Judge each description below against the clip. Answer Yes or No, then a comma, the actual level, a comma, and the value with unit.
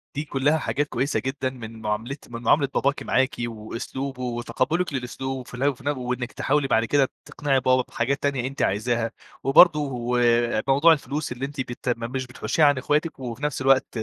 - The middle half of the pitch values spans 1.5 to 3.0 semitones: Yes, average, 2.7 semitones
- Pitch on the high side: No, low, 130 Hz